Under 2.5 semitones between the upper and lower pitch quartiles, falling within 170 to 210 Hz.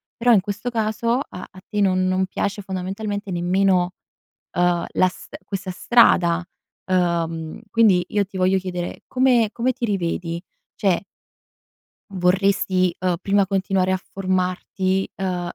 Yes: narrow, 2.0 semitones; high, 190 Hz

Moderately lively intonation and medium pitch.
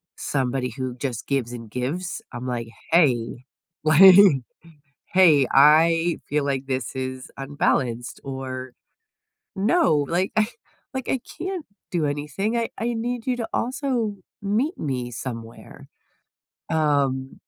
No: wide, 7.0 semitones; medium, 145 Hz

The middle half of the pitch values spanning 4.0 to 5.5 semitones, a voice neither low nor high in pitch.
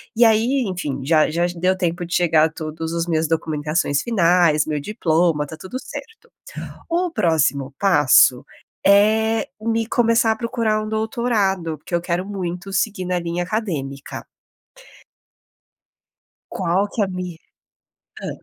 Yes: average, 5.1 semitones; medium, 180 Hz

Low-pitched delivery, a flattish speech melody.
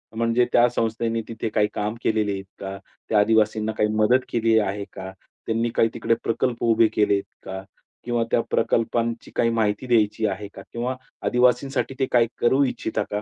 Yes: low, 115 Hz; narrow, 1.9 semitones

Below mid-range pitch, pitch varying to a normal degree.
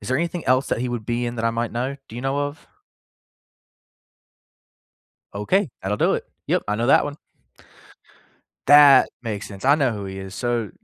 Yes: low, 120 Hz; average, 4.2 semitones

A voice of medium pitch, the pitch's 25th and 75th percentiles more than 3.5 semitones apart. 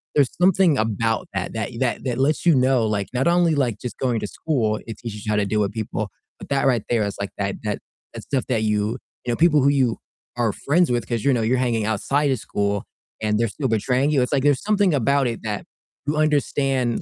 No: low, 125 Hz; average, 4.5 semitones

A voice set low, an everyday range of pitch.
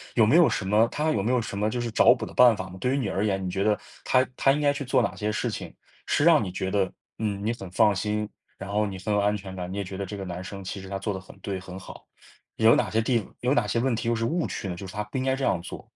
Yes: low, 105 Hz; average, 3.7 semitones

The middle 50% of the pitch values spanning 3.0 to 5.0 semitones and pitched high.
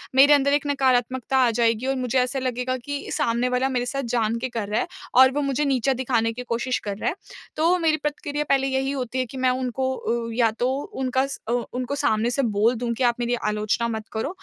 No: narrow, 2.5 semitones; very high, 255 Hz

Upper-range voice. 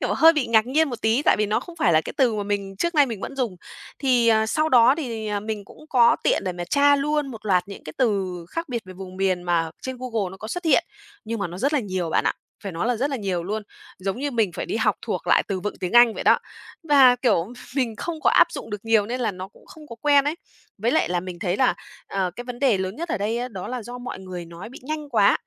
Yes: high, 225 Hz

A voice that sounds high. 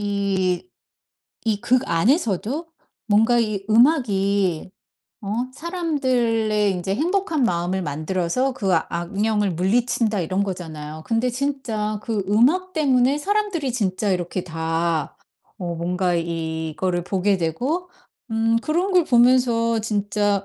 Yes: high, 210 Hz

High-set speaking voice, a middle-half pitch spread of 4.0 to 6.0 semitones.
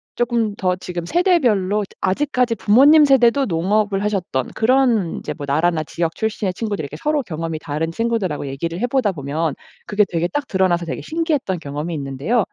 No: high, 195 Hz; wide, 6.4 semitones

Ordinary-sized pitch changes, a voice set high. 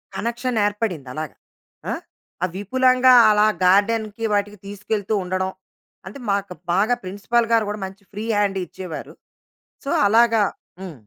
Yes: average, 3.1 semitones; high, 205 Hz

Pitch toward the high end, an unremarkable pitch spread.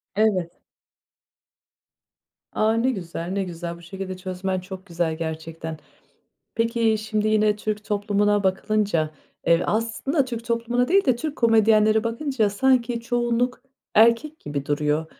Yes: high, 215 Hz; average, 4.3 semitones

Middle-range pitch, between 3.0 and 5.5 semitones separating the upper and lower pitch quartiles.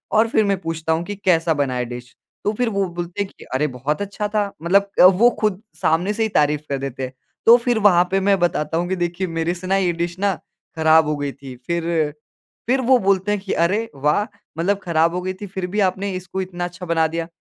Yes: medium, 180 Hz; average, 3.8 semitones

